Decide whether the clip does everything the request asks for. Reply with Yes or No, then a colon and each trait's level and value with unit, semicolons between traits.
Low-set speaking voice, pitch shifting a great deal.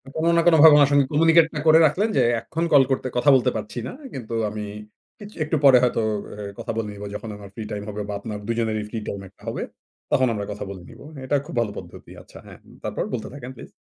Yes: low, 130 Hz; wide, 6.1 semitones